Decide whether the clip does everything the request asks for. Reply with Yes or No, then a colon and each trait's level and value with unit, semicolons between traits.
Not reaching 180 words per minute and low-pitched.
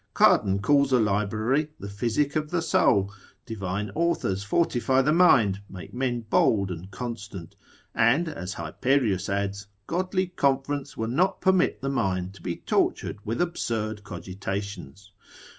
Yes: average, 140 wpm; low, 110 Hz